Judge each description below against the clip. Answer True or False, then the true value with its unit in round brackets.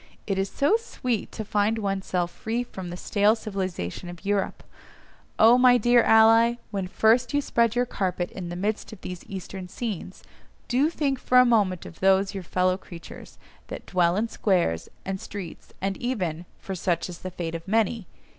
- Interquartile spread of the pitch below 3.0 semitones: False (4.0 semitones)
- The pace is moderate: True (185 wpm)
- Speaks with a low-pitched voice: False (195 Hz)